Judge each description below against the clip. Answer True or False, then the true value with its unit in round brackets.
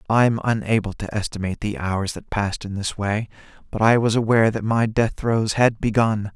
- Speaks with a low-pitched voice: True (110 Hz)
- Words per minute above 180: True (200 wpm)